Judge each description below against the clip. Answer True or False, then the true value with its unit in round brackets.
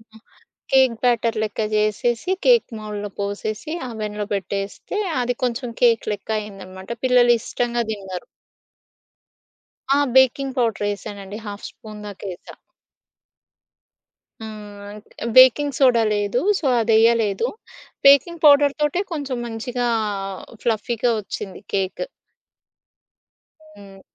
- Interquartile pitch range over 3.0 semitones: True (3.4 semitones)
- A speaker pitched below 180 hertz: False (225 Hz)